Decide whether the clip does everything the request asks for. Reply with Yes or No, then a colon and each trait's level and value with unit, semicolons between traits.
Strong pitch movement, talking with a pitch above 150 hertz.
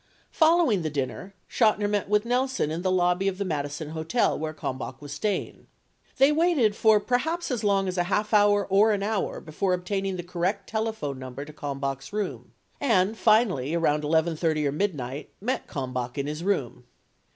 Yes: wide, 6.0 semitones; medium, 185 Hz